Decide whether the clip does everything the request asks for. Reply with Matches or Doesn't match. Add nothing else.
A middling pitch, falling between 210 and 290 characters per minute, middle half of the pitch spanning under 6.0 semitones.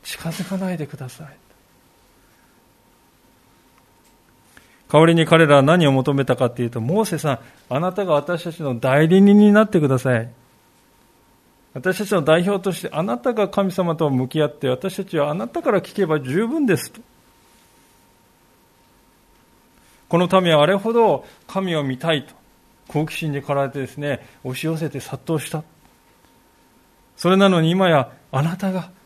Matches